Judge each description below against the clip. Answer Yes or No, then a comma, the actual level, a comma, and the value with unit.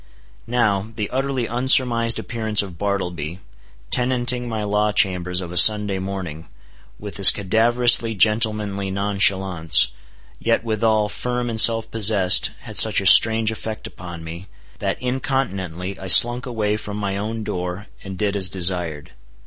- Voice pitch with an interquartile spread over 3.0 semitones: Yes, average, 3.4 semitones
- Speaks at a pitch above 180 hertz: No, low, 105 Hz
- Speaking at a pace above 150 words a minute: No, average, 140 wpm